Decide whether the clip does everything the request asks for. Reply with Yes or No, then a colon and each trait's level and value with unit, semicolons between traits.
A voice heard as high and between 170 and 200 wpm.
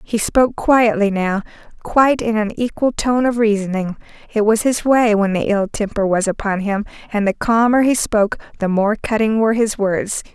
Yes: high, 215 Hz; average, 190 wpm